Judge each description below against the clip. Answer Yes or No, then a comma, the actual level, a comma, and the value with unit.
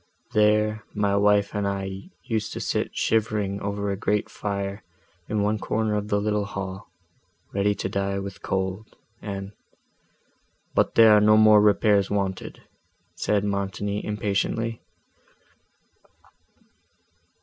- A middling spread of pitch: No, narrow, 1.3 semitones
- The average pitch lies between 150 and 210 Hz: No, low, 105 Hz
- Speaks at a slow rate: Yes, slow, 125 wpm